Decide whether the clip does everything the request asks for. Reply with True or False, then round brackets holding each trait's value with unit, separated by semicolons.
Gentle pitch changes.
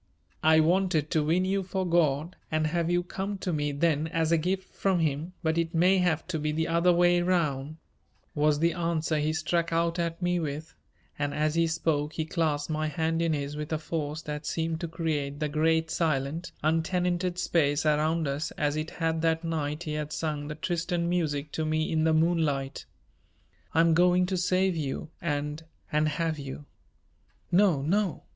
True (2.2 semitones)